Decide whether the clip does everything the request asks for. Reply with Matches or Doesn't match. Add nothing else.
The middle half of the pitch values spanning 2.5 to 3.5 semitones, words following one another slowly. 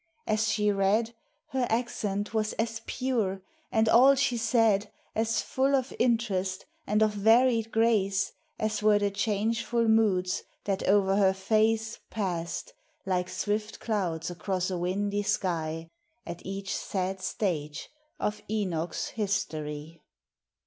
Matches